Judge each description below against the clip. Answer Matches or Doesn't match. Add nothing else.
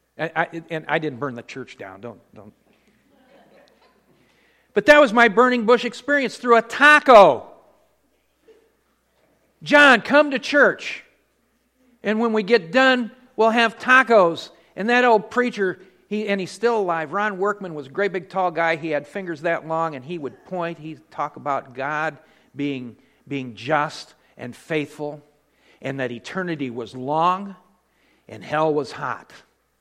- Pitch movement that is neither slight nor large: Doesn't match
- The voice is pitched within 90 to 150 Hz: Doesn't match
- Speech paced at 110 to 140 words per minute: Doesn't match